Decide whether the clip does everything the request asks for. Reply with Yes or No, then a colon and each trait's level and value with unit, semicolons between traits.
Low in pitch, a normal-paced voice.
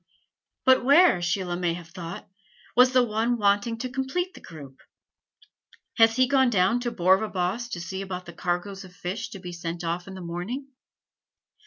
No: high, 195 Hz; average, 175 wpm